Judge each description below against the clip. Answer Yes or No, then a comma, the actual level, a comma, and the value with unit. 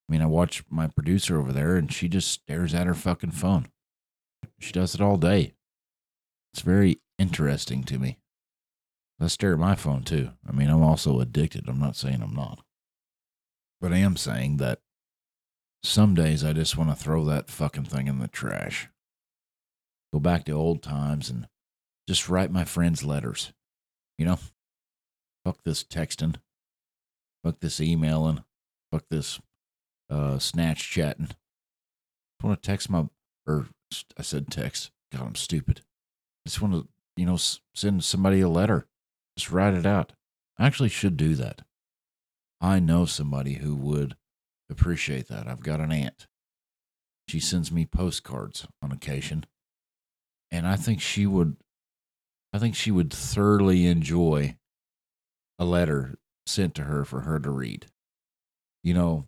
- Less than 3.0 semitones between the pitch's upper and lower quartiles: No, average, 4.2 semitones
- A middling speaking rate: Yes, average, 155 wpm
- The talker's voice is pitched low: Yes, very low, 80 Hz